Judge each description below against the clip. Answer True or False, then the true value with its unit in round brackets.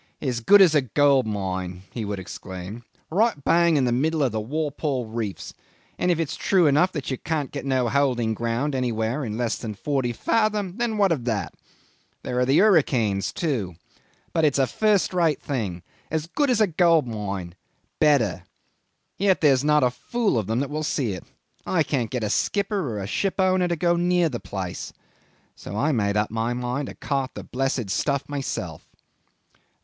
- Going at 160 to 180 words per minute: False (190 wpm)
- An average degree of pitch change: False (6.5 semitones)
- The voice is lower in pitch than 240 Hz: True (135 Hz)